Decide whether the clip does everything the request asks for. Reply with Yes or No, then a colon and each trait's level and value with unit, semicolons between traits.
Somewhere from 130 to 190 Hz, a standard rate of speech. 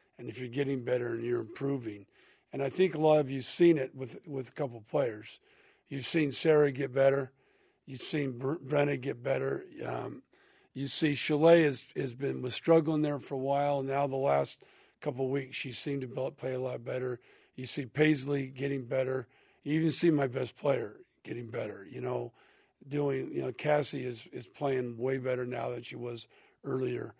Yes: low, 135 Hz; average, 195 wpm